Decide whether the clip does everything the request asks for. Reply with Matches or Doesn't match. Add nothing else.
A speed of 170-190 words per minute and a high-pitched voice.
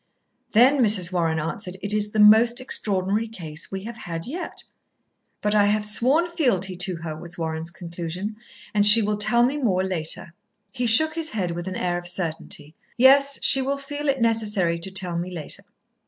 Matches